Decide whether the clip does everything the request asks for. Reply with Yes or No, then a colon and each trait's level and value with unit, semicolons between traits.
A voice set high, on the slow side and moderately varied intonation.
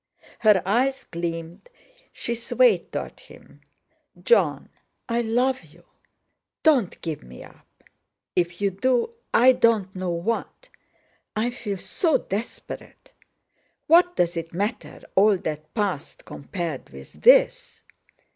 No: high, 210 Hz; slow, 110 wpm; wide, 6.7 semitones